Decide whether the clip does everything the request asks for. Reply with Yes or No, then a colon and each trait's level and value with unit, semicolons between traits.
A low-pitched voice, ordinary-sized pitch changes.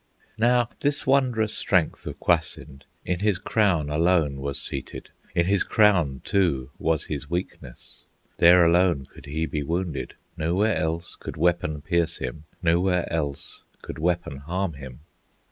Yes: very low, 85 Hz; average, 3.9 semitones